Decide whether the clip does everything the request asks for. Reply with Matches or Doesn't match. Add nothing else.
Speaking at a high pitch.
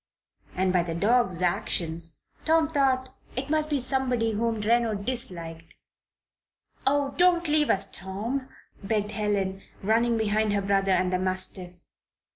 Matches